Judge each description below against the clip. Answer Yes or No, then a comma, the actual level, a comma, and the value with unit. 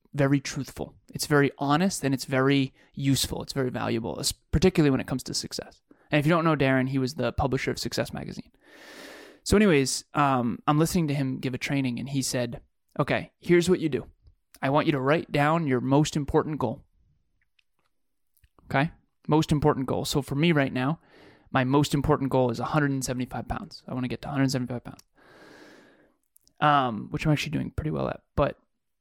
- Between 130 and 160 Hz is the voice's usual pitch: Yes, medium, 140 Hz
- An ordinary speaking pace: Yes, average, 190 wpm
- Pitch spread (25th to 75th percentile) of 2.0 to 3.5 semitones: Yes, average, 2.8 semitones